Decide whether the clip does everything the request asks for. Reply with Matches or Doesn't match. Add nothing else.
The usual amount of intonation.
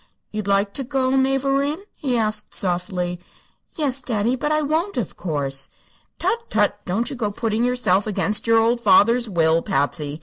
Doesn't match